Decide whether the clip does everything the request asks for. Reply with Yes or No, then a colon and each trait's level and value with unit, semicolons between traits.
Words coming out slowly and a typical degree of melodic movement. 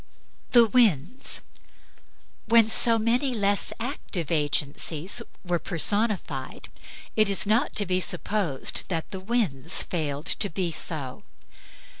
No: slow, 115 wpm; wide, 5.7 semitones